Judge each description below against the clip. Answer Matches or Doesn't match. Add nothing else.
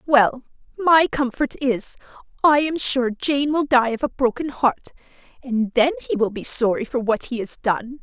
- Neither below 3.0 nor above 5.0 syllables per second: Matches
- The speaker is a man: Doesn't match